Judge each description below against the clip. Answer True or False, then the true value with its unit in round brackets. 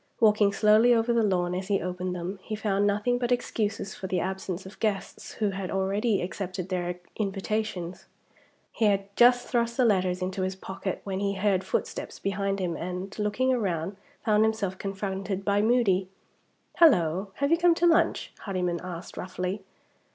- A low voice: False (195 Hz)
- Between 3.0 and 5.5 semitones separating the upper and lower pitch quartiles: False (2.6 semitones)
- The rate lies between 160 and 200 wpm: True (170 wpm)